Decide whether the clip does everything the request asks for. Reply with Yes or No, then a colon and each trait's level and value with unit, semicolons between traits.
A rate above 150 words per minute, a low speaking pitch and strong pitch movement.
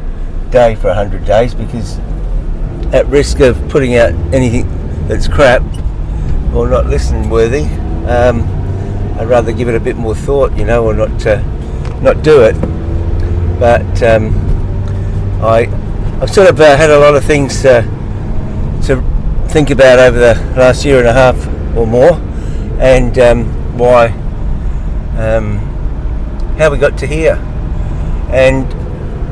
No: average, 145 wpm; low, 110 Hz; wide, 6.0 semitones